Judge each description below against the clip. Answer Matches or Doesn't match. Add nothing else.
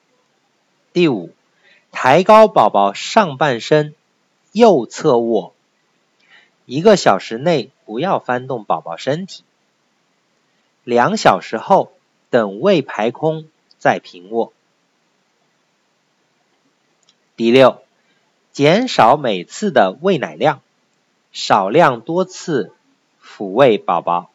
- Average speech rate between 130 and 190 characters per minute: Matches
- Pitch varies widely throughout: Matches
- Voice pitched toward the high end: Doesn't match